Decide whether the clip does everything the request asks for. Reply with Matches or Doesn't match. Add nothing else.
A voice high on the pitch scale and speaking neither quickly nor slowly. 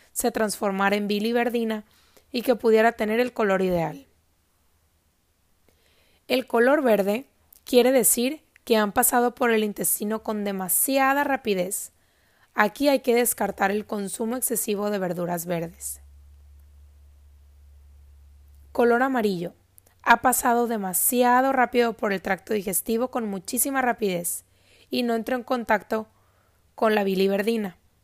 Doesn't match